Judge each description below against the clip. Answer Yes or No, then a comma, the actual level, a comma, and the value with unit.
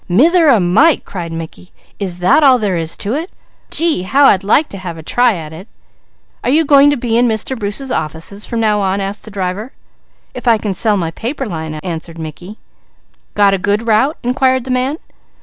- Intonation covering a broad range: Yes, wide, 6.1 semitones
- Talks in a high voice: Yes, high, 210 Hz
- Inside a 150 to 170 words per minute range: No, fast, 205 wpm